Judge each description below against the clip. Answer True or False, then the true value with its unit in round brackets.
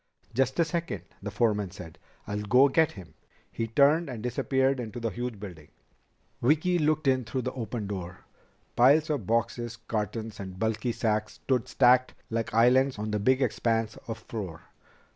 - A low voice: True (115 Hz)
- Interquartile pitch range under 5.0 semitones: True (3.9 semitones)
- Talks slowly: False (165 wpm)